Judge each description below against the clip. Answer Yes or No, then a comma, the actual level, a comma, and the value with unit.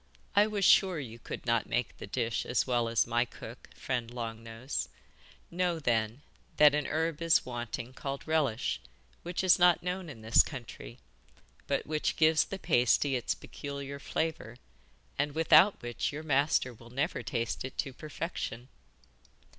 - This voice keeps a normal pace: Yes, average, 160 wpm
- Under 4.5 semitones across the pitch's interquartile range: No, average, 5.1 semitones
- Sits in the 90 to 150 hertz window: Yes, low, 135 Hz